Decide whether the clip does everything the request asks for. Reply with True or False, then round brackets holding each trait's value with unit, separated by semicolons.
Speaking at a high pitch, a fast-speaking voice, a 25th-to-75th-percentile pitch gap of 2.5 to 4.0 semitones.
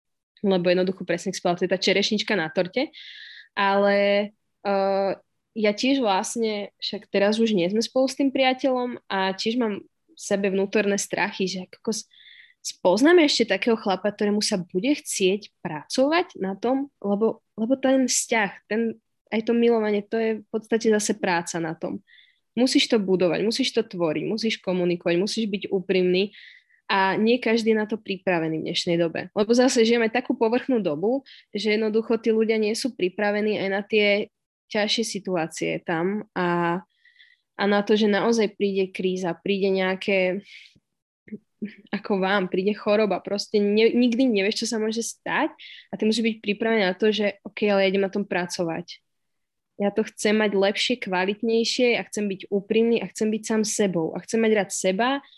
True (210 Hz; 170 wpm; 2.9 semitones)